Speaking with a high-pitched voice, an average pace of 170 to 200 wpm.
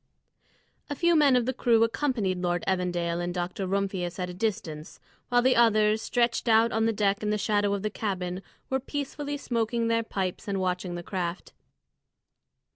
Yes: high, 210 Hz; average, 180 wpm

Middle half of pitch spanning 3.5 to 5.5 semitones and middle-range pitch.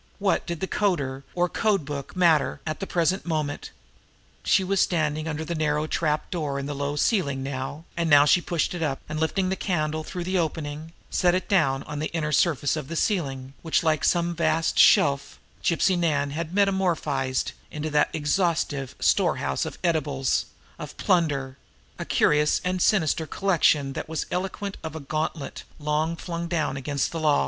No: average, 3.1 semitones; medium, 155 Hz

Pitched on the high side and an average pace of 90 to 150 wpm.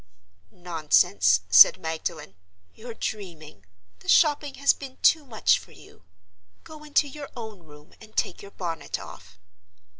Yes: high, 200 Hz; average, 140 wpm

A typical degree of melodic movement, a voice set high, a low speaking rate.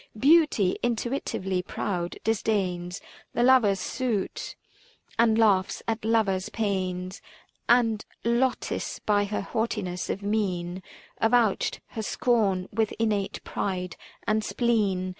Yes: average, 3.4 semitones; high, 210 Hz; slow, 105 wpm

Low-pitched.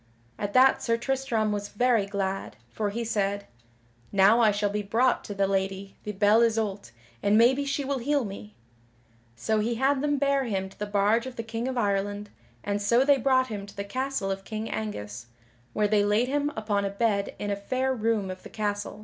No: high, 215 Hz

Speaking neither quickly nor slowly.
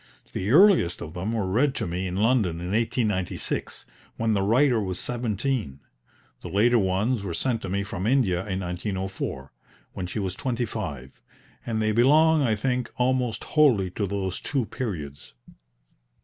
Yes: average, 165 wpm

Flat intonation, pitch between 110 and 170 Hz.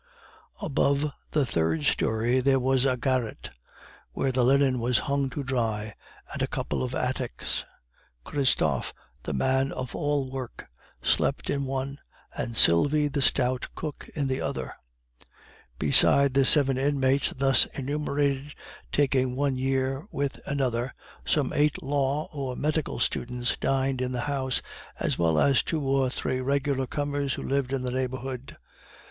Yes: narrow, 1.8 semitones; low, 135 Hz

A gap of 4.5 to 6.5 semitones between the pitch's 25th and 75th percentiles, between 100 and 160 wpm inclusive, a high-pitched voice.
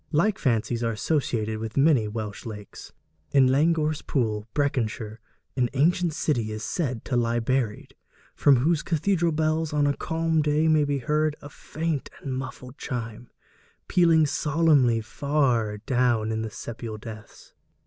No: average, 5.3 semitones; average, 150 wpm; low, 135 Hz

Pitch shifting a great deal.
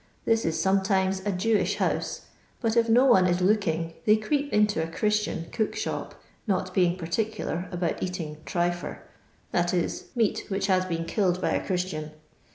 No: average, 3.3 semitones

